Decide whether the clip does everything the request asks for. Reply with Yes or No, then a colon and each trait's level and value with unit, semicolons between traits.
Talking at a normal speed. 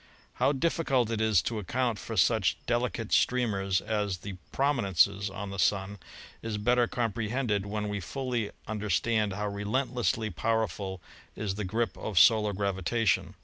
Yes: average, 155 wpm